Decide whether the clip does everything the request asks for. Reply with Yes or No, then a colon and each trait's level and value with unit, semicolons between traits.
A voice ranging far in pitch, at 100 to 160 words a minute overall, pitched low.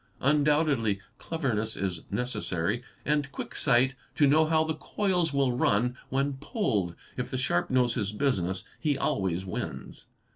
Yes: wide, 6.1 semitones; average, 145 wpm; low, 130 Hz